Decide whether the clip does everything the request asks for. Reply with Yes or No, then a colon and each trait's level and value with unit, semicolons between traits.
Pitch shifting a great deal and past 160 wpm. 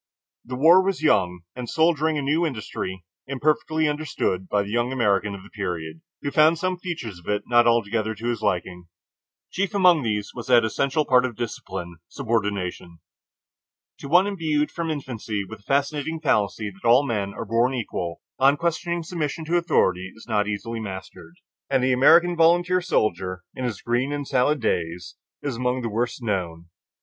Yes: wide, 6.9 semitones; average, 175 wpm